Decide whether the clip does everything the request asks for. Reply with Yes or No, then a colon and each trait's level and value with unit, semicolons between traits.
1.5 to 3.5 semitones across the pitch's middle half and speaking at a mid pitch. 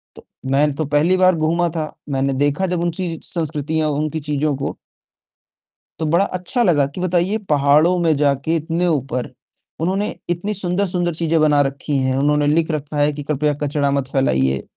Yes: average, 3.2 semitones; medium, 155 Hz